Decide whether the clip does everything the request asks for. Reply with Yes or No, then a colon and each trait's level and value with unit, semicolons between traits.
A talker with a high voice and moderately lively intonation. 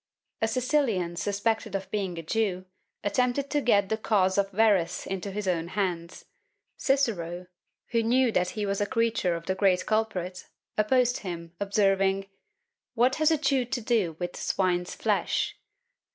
Yes: high, 200 Hz; average, 3.9 semitones